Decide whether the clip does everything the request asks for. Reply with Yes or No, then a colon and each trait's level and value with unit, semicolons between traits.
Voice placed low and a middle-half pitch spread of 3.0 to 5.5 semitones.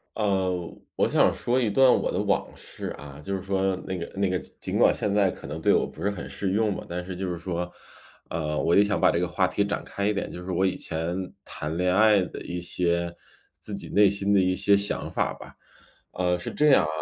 No: very low, 95 Hz; narrow, 2.4 semitones